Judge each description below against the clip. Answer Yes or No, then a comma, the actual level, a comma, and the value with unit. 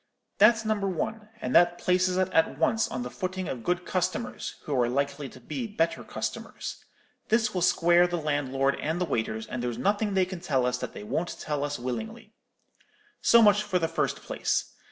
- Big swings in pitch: Yes, wide, 6.3 semitones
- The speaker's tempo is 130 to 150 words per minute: No, average, 195 wpm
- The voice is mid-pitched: Yes, medium, 175 Hz